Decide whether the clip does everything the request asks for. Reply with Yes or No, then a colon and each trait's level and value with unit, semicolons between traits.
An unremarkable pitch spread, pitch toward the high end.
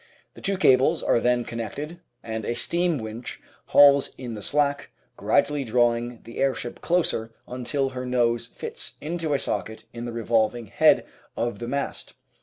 No: average, 3.4 semitones; low, 125 Hz